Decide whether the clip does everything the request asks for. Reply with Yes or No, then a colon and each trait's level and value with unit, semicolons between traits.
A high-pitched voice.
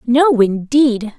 Yes: high, 245 Hz